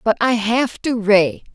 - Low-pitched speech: No, high, 220 Hz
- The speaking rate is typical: Yes, average, 195 wpm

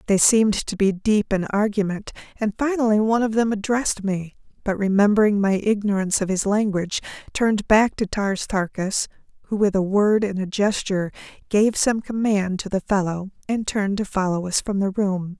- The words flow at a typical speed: Yes, average, 180 wpm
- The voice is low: No, high, 205 Hz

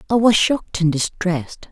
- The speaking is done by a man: No, female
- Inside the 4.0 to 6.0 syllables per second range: Yes, 5.4 syllables/s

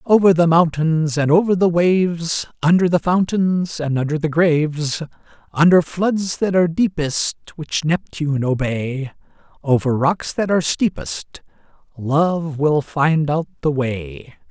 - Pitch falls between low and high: Yes, medium, 160 Hz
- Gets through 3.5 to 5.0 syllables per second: Yes, 4.1 syllables/s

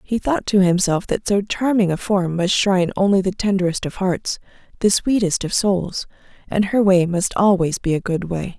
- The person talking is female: Yes, female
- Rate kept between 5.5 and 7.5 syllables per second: No, 4.9 syllables/s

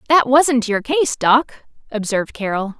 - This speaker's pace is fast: No, average, 150 wpm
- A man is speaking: No, female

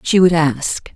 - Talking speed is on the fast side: No, average, 190 wpm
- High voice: No, medium, 165 Hz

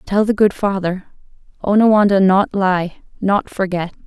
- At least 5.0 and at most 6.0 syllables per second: No, 4.5 syllables/s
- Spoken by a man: No, female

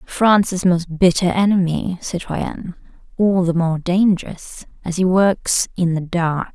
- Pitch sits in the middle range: Yes, medium, 180 Hz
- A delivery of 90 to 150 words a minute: Yes, average, 140 wpm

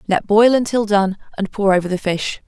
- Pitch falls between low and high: No, high, 205 Hz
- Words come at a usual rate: No, fast, 220 wpm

